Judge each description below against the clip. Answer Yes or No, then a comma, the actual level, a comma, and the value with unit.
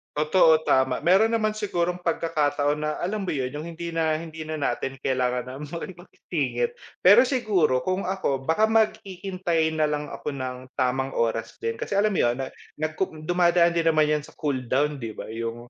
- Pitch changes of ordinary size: Yes, average, 5.0 semitones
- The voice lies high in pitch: No, medium, 155 Hz